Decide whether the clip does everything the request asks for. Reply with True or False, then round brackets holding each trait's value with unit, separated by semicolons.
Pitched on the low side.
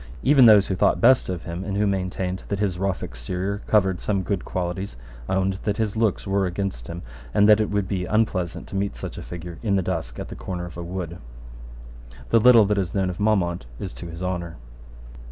True (95 Hz)